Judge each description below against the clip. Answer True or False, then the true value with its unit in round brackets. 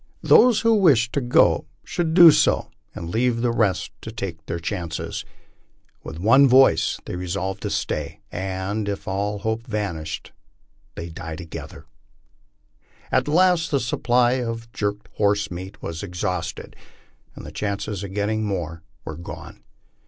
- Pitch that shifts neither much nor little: True (4.9 semitones)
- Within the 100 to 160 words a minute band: True (145 wpm)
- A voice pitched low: True (105 Hz)